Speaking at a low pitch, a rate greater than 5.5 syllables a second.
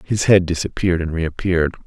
Yes: very low, 85 Hz; 6.0 syllables/s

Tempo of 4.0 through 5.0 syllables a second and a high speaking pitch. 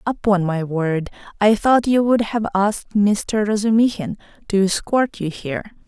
Yes: 4.7 syllables/s; high, 205 Hz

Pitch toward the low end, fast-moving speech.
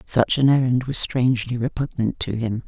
No: low, 125 Hz; average, 180 wpm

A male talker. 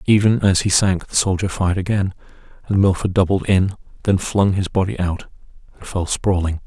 Yes: male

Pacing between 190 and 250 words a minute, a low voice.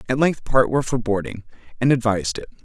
Yes: fast, 205 wpm; low, 125 Hz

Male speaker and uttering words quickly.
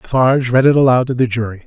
Yes: male; fast, 250 wpm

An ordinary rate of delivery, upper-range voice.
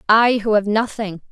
Yes: average, 180 wpm; high, 215 Hz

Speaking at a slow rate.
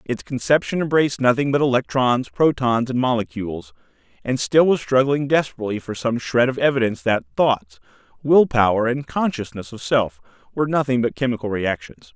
No: average, 160 wpm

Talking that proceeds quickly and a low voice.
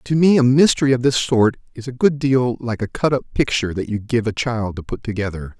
Yes: fast, 255 wpm; low, 120 Hz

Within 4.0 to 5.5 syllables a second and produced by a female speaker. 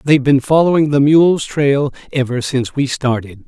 No: 5.1 syllables/s; male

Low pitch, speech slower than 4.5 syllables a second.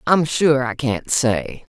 Yes: low, 130 Hz; 3.3 syllables/s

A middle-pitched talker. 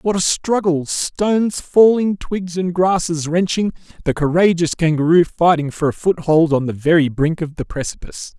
Yes: medium, 170 Hz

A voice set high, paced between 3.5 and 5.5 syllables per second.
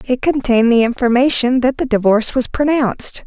No: very high, 250 Hz; 5.8 syllables/s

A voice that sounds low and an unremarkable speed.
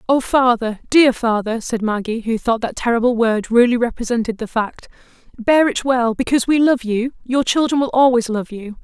No: high, 240 Hz; average, 190 wpm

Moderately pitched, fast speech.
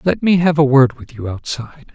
Yes: medium, 145 Hz; fast, 245 wpm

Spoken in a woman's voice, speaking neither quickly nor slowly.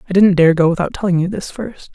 No: female; fast, 280 wpm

